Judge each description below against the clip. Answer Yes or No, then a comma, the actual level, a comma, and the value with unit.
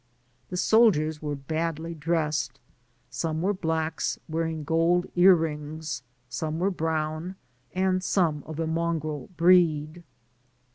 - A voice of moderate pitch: Yes, medium, 160 Hz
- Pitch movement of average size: No, narrow, 2.1 semitones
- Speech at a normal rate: No, slow, 115 wpm